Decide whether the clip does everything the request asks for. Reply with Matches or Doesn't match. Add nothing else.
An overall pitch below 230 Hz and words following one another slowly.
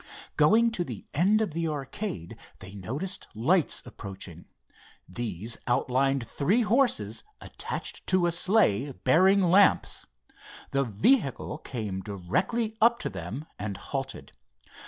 Matches